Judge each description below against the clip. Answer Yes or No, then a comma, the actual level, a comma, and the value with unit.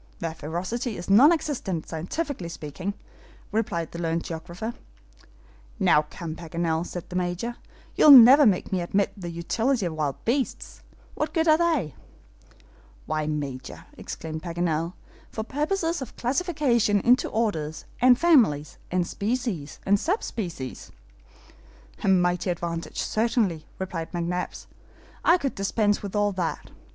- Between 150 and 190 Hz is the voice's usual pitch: Yes, medium, 185 Hz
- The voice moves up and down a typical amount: No, wide, 6.3 semitones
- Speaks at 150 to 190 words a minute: No, slow, 135 wpm